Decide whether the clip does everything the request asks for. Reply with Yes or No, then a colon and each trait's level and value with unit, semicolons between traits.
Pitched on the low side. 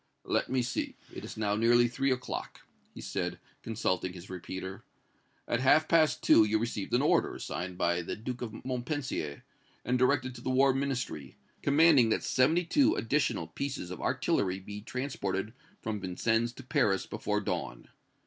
Yes: low, 120 Hz